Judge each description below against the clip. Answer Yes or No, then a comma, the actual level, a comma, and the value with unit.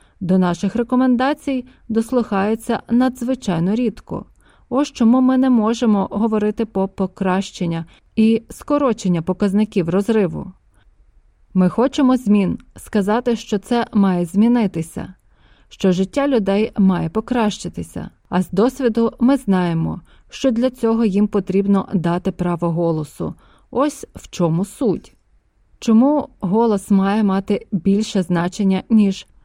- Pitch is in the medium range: No, high, 210 Hz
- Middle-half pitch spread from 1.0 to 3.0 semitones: No, average, 3.7 semitones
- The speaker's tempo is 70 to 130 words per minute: Yes, average, 110 wpm